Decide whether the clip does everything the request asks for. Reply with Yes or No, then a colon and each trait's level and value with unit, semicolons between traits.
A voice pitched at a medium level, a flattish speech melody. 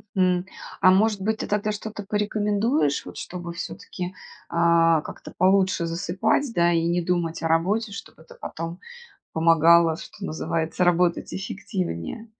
No: medium, 180 Hz; average, 3.5 semitones